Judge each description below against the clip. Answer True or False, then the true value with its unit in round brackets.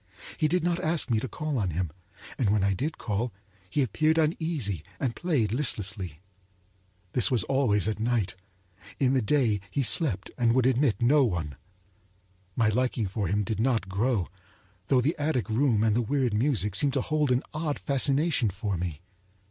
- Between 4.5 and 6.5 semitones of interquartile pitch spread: True (5.6 semitones)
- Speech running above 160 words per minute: True (175 wpm)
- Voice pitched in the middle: False (120 Hz)